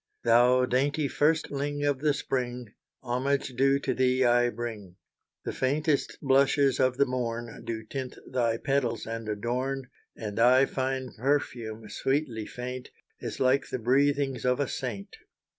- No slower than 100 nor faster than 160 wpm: Yes, average, 140 wpm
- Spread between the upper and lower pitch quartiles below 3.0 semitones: Yes, narrow, 2.4 semitones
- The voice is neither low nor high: No, low, 130 Hz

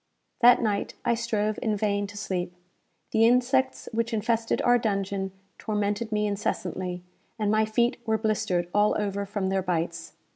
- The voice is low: No, high, 210 Hz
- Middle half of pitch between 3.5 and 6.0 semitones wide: No, narrow, 2.4 semitones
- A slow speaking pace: No, average, 155 wpm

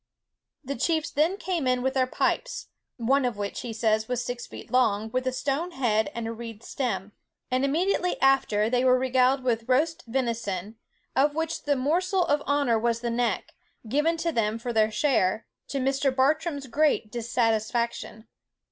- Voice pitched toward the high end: Yes, very high, 255 Hz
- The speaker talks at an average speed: Yes, average, 175 wpm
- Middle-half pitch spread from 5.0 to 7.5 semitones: No, average, 3.9 semitones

